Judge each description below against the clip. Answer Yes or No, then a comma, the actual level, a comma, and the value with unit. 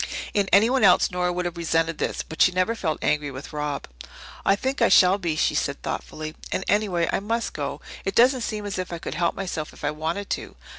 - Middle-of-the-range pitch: Yes, medium, 180 Hz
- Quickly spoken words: Yes, fast, 230 wpm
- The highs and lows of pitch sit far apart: No, average, 4.2 semitones